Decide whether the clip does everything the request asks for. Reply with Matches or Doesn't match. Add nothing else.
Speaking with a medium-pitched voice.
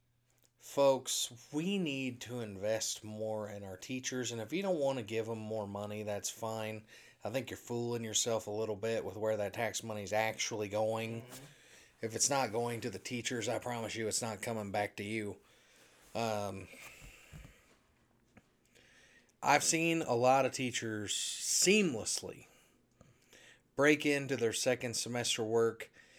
Doesn't match